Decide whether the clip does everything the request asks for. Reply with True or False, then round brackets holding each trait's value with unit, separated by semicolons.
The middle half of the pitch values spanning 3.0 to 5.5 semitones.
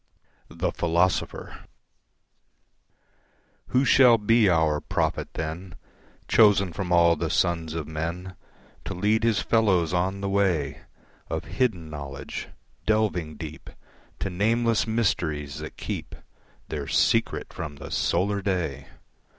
True (4.4 semitones)